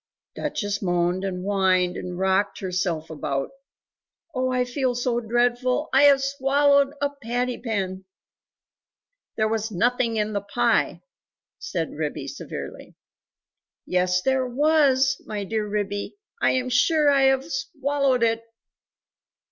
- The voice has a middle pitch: No, high, 240 Hz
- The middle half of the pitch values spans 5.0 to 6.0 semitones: Yes, wide, 5.4 semitones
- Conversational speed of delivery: No, slow, 125 wpm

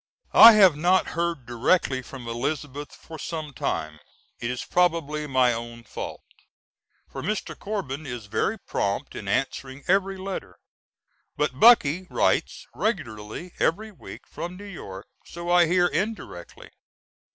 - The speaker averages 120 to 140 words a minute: Yes, slow, 135 wpm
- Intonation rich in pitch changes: Yes, wide, 6.9 semitones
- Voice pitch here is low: No, medium, 150 Hz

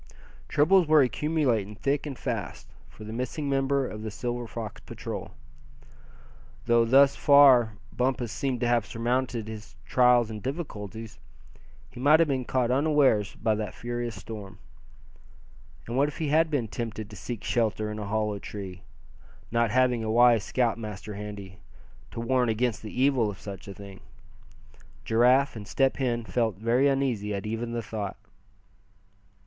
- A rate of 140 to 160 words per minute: Yes, average, 155 wpm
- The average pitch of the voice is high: No, low, 120 Hz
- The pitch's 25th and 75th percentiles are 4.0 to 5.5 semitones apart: No, average, 3.6 semitones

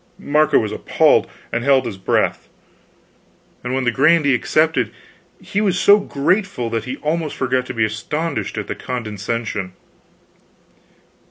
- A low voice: Yes, low, 130 Hz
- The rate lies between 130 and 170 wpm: Yes, average, 140 wpm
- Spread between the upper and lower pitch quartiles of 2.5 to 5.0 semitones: No, wide, 5.4 semitones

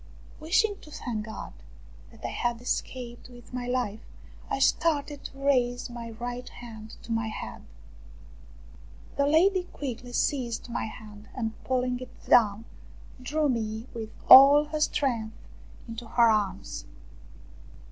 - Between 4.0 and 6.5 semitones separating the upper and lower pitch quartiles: No, average, 3.4 semitones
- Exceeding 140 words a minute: No, slow, 135 wpm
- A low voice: No, high, 245 Hz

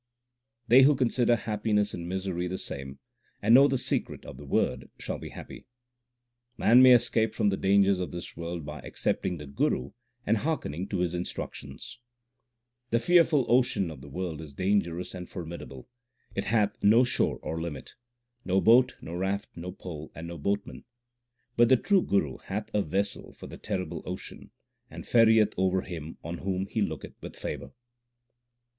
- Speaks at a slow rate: No, average, 175 wpm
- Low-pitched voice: Yes, very low, 95 Hz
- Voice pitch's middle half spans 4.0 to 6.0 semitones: Yes, average, 5.0 semitones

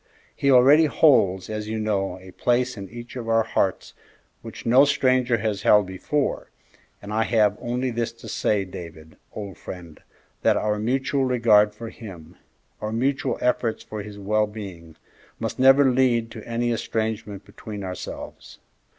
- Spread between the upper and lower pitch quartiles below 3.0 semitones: No, average, 3.4 semitones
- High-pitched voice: No, low, 110 Hz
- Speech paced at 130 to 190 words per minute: Yes, average, 160 wpm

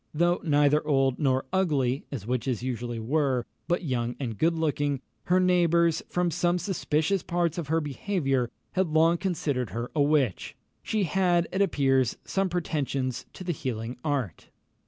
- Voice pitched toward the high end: No, medium, 150 Hz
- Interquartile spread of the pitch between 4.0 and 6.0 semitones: Yes, average, 5.0 semitones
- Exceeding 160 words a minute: No, average, 155 wpm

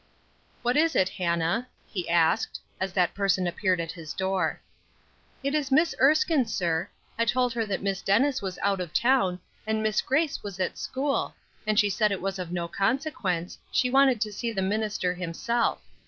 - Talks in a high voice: Yes, high, 200 Hz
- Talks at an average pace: Yes, average, 185 wpm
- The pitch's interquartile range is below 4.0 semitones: No, wide, 5.5 semitones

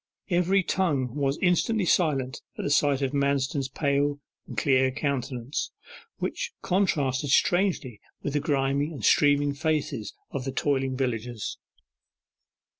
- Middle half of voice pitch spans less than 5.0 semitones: Yes, average, 2.7 semitones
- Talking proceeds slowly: Yes, slow, 125 wpm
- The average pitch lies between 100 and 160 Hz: Yes, medium, 140 Hz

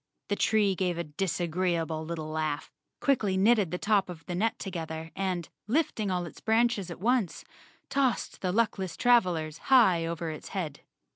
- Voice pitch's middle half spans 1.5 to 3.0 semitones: No, average, 4.5 semitones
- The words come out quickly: No, average, 160 wpm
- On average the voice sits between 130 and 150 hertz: No, medium, 185 Hz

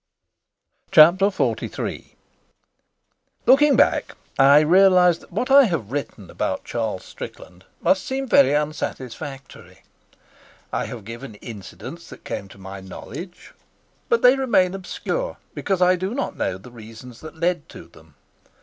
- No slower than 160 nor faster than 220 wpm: No, slow, 135 wpm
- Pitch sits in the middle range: Yes, medium, 155 Hz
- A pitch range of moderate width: No, wide, 9.0 semitones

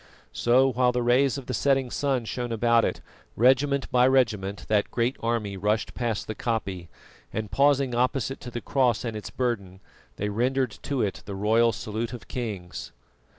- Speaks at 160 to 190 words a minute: Yes, average, 175 wpm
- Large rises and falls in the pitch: No, average, 3.3 semitones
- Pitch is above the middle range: No, low, 120 Hz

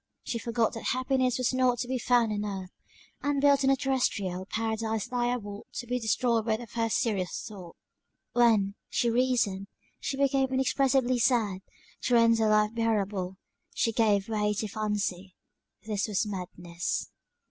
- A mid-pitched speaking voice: No, high, 225 Hz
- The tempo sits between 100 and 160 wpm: Yes, average, 150 wpm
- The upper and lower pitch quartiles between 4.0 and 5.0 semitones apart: No, average, 3.3 semitones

